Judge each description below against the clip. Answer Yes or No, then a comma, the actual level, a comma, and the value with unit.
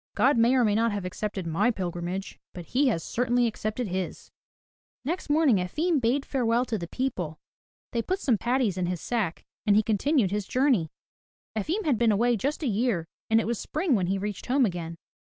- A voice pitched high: Yes, high, 225 Hz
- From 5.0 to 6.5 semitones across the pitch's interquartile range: Yes, average, 5.3 semitones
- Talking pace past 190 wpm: Yes, average, 200 wpm